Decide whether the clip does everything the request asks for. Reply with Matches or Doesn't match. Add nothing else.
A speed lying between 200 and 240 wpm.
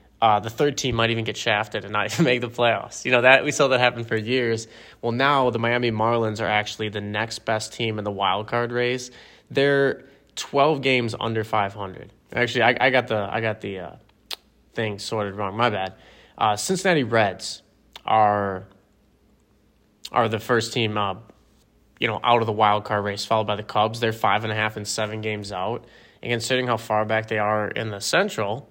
Matches